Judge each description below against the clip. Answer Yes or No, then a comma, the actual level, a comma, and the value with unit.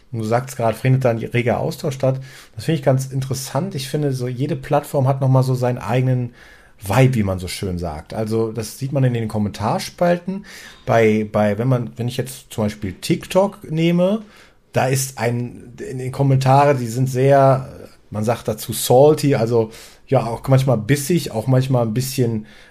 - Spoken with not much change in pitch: No, average, 3.3 semitones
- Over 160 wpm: Yes, fast, 190 wpm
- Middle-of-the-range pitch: No, low, 130 Hz